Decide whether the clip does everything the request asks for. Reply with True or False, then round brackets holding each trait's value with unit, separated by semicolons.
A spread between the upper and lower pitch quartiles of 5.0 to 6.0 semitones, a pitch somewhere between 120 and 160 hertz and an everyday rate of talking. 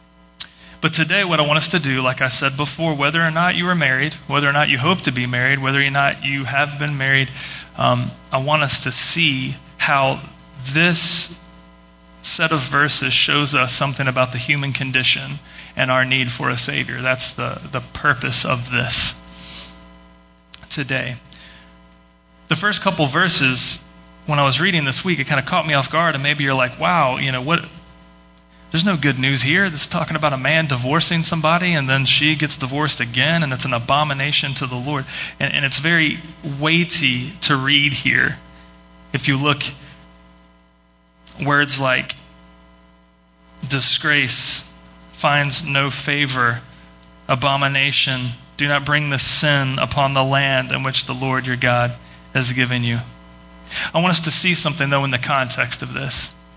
False (3.6 semitones; 135 Hz; 170 wpm)